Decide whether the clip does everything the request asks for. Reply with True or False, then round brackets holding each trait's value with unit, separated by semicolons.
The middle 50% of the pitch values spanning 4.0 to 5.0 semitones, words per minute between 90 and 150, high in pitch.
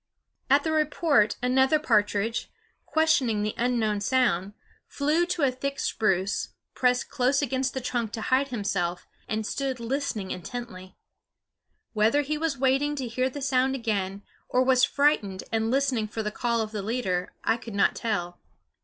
False (4.4 semitones; 160 wpm; 245 Hz)